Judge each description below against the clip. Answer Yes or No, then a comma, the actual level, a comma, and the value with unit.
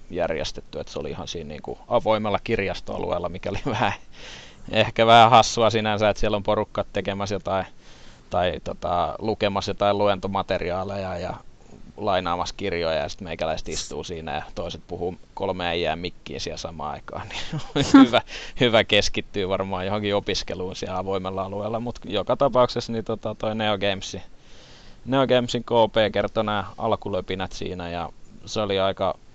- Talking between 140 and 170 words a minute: Yes, average, 150 wpm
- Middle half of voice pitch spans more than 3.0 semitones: No, narrow, 2.5 semitones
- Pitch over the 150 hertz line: No, low, 100 Hz